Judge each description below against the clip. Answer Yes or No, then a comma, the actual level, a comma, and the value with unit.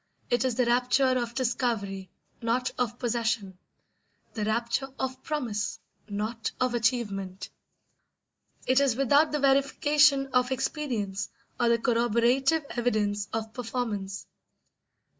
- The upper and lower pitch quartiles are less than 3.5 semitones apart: Yes, average, 3.1 semitones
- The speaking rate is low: Yes, slow, 115 wpm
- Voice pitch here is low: No, high, 240 Hz